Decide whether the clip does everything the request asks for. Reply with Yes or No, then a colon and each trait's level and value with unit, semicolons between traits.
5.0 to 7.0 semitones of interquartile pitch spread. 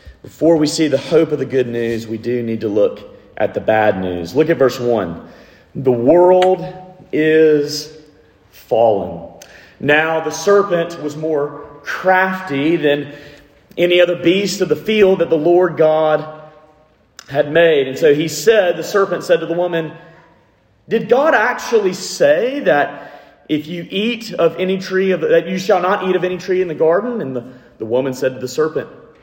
No: average, 3.9 semitones